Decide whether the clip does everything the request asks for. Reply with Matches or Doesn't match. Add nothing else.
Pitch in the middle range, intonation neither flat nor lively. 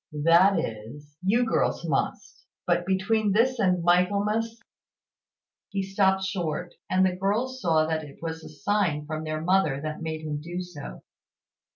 Matches